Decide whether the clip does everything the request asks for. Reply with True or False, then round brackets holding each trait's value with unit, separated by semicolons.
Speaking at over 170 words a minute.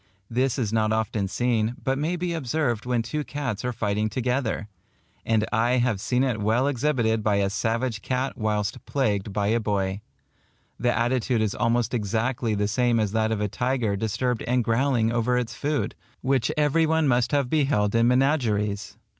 True (180 wpm)